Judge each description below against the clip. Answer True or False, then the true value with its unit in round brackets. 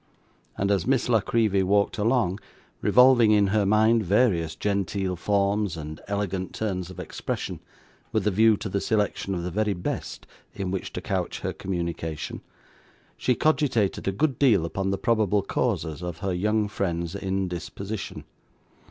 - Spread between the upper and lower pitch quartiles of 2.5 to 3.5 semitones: True (2.8 semitones)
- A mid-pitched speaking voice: False (100 Hz)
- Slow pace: False (155 wpm)